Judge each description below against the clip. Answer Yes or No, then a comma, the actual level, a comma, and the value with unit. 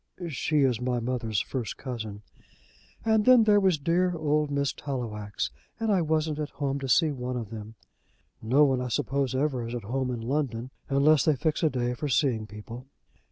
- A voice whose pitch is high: No, low, 135 Hz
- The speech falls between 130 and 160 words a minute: No, average, 190 wpm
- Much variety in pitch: No, average, 4.0 semitones